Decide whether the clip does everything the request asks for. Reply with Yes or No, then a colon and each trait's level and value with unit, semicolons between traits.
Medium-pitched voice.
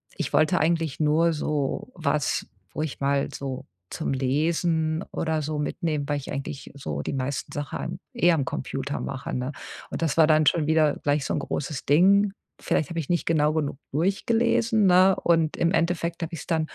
Yes: medium, 155 Hz